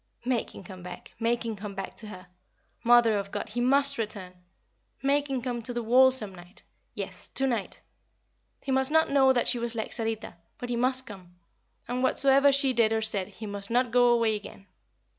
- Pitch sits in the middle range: No, high, 235 Hz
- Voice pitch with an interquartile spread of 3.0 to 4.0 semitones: Yes, average, 3.7 semitones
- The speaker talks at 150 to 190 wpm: No, fast, 205 wpm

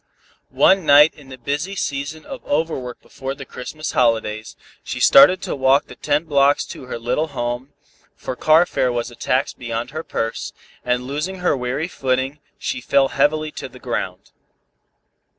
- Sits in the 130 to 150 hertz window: Yes, medium, 140 Hz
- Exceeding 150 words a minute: Yes, average, 170 wpm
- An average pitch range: Yes, average, 3.6 semitones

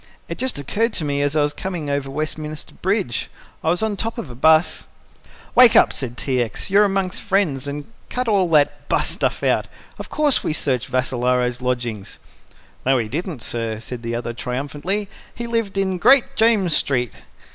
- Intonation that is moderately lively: No, wide, 7.6 semitones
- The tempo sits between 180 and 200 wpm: Yes, average, 190 wpm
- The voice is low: No, medium, 150 Hz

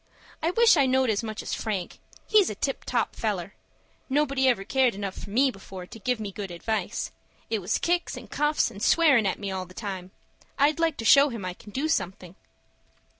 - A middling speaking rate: No, fast, 210 wpm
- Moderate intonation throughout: No, wide, 6.2 semitones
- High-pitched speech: Yes, high, 225 Hz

